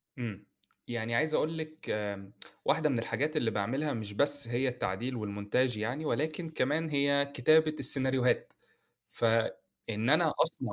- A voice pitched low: Yes, low, 130 Hz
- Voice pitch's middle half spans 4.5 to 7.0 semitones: Yes, average, 5.2 semitones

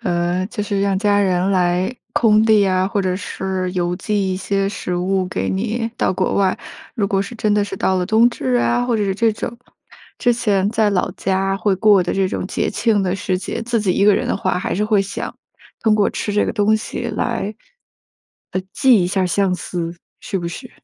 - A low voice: No, high, 195 Hz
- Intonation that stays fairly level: Yes, narrow, 2.3 semitones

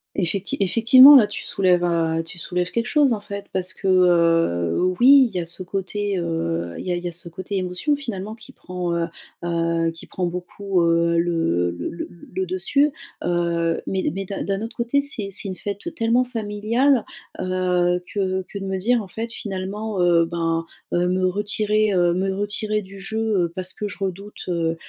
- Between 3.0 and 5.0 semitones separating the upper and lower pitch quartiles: Yes, average, 3.3 semitones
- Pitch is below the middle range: No, medium, 185 Hz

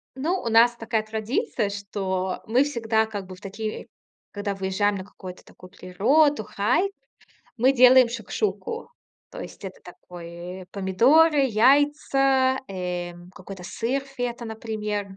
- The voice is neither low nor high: No, high, 220 Hz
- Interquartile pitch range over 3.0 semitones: Yes, wide, 5.4 semitones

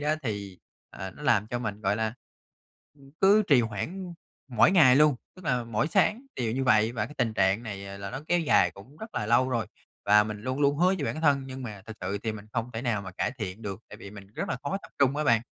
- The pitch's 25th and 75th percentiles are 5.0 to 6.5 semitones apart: Yes, average, 5.3 semitones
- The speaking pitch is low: Yes, low, 115 Hz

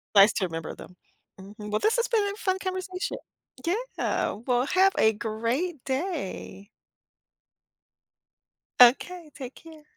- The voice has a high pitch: Yes, very high, 290 Hz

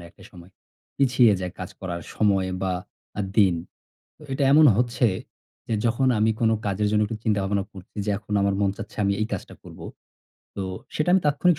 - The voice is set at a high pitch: No, low, 105 Hz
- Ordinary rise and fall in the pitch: Yes, average, 3.7 semitones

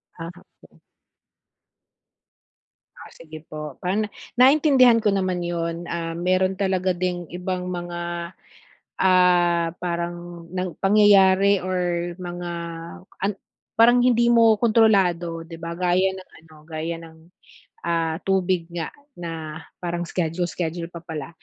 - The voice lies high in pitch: No, medium, 175 Hz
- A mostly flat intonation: Yes, narrow, 2.1 semitones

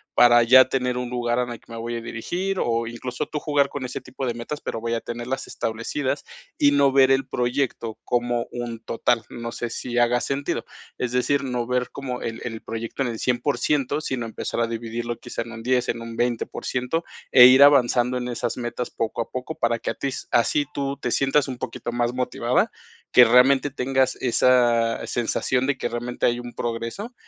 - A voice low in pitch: Yes, low, 125 Hz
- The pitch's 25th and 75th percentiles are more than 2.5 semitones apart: No, narrow, 2.0 semitones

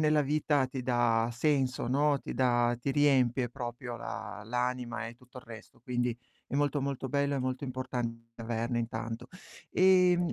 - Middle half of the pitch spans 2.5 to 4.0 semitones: Yes, average, 2.9 semitones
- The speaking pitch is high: No, low, 125 Hz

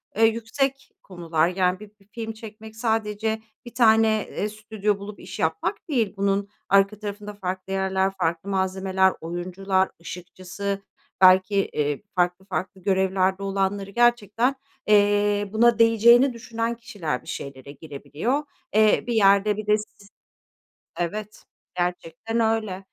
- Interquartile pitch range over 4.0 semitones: No, average, 2.8 semitones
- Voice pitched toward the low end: No, high, 200 Hz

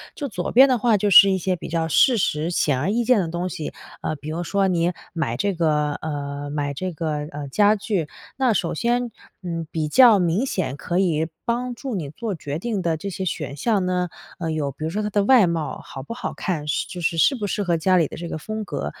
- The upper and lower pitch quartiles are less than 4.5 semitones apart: No, average, 5.0 semitones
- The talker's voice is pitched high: No, medium, 175 Hz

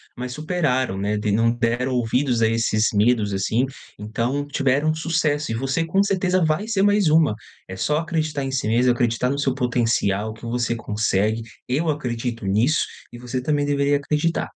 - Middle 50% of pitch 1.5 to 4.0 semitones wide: No, average, 4.8 semitones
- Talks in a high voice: No, low, 125 Hz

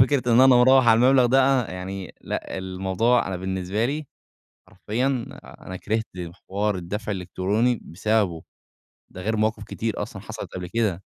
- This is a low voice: Yes, low, 105 Hz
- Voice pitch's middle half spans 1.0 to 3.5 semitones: No, average, 4.4 semitones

